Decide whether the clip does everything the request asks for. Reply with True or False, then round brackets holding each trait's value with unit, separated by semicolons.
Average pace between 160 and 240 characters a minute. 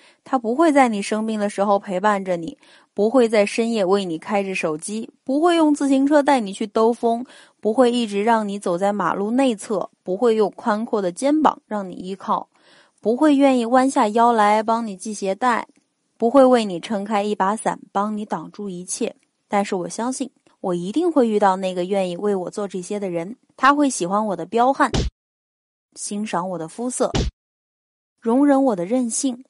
False (265 characters per minute)